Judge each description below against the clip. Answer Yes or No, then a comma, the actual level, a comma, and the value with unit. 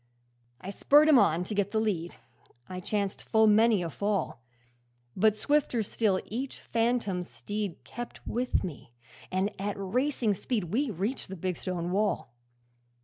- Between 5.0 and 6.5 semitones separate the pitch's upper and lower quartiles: No, average, 3.8 semitones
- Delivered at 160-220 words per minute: No, average, 150 wpm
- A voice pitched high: Yes, high, 205 Hz